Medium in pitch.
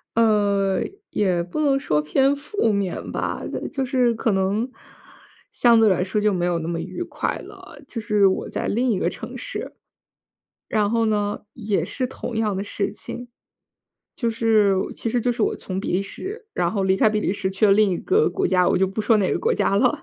No: high, 210 Hz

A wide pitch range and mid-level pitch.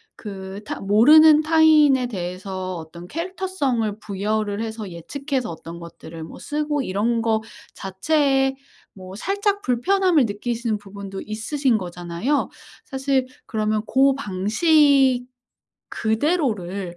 No: wide, 6.6 semitones; high, 225 Hz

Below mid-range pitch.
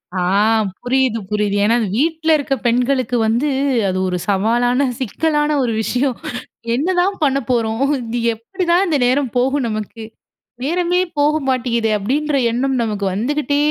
No: very high, 255 Hz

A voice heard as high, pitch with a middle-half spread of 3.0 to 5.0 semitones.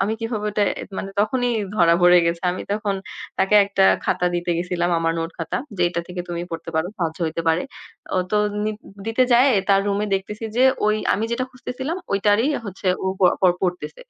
Yes: high, 195 Hz; average, 3.6 semitones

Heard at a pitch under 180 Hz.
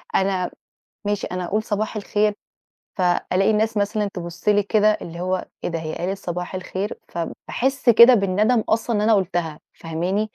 No: high, 200 Hz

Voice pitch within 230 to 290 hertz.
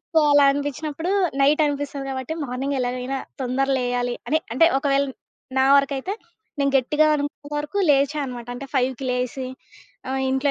Yes: very high, 275 Hz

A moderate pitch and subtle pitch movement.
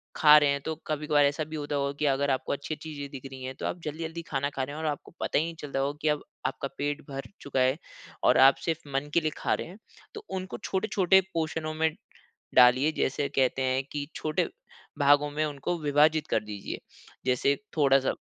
Yes: medium, 145 Hz; narrow, 2.3 semitones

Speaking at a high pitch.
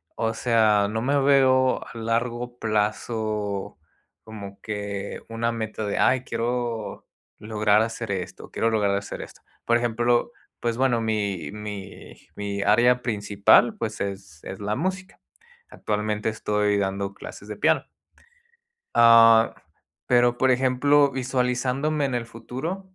No: low, 115 Hz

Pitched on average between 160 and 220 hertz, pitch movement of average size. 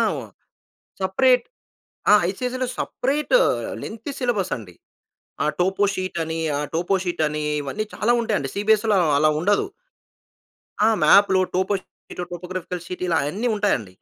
Yes: high, 190 Hz; average, 4.2 semitones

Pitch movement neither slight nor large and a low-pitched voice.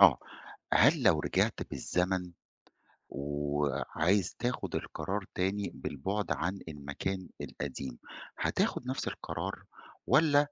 No: wide, 5.7 semitones; very low, 90 Hz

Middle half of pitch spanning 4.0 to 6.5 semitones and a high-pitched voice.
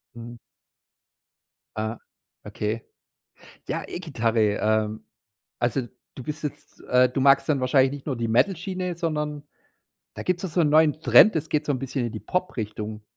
No: average, 5.0 semitones; low, 135 Hz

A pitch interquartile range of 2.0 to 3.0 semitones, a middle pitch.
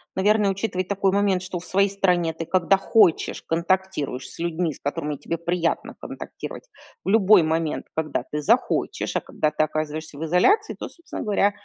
No: average, 3.7 semitones; medium, 180 Hz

